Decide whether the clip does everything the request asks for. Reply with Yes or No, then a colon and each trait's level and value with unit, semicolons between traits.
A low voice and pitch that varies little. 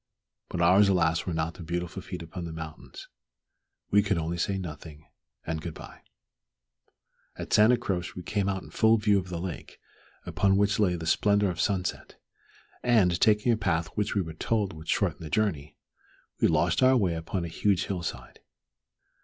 No: very low, 90 Hz; average, 3.6 semitones